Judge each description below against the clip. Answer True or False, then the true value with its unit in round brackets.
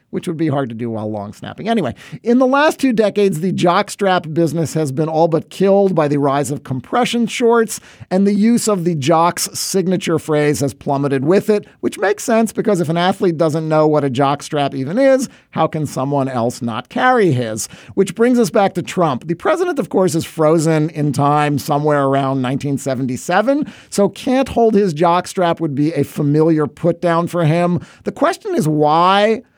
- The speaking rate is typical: True (195 wpm)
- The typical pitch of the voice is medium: True (165 Hz)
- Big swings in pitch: True (5.7 semitones)